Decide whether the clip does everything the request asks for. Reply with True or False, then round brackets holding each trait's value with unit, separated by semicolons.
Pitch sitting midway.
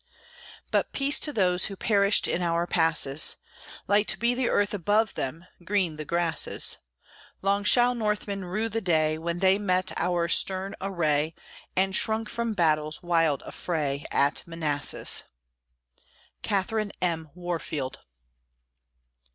True (180 Hz)